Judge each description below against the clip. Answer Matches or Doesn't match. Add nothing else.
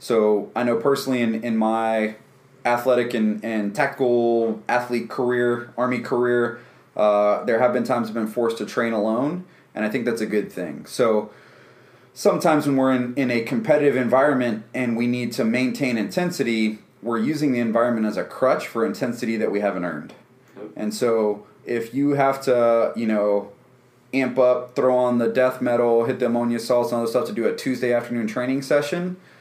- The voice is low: Matches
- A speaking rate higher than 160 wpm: Matches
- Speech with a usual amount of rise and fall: Doesn't match